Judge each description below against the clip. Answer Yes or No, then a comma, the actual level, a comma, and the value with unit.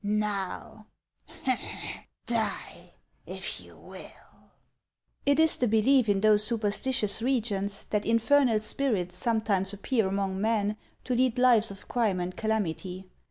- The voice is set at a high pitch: Yes, high, 215 Hz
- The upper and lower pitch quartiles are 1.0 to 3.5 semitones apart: Yes, average, 3.0 semitones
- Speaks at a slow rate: Yes, slow, 125 wpm